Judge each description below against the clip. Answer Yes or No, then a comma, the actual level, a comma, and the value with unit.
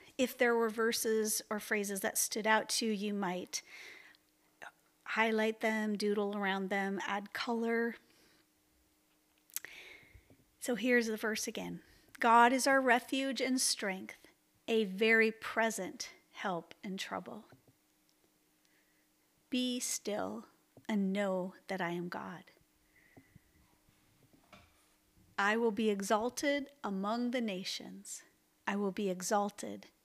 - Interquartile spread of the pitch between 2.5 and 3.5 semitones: Yes, average, 3.1 semitones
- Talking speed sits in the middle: No, slow, 110 wpm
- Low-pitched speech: No, high, 220 Hz